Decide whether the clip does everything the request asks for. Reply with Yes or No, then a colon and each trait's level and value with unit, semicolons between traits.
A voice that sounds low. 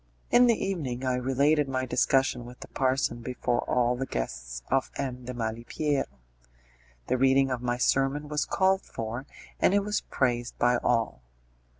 Yes: low, 130 Hz